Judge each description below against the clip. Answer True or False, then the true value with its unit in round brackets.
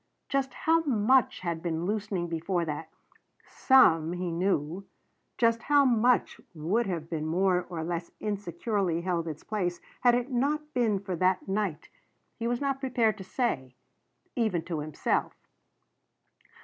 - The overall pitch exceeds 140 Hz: True (190 Hz)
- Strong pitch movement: True (6.0 semitones)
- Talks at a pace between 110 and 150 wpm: True (140 wpm)